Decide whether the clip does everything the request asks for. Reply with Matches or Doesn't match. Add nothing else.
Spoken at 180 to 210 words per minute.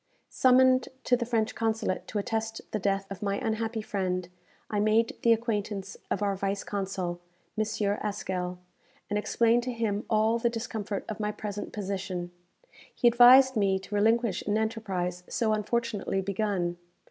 Doesn't match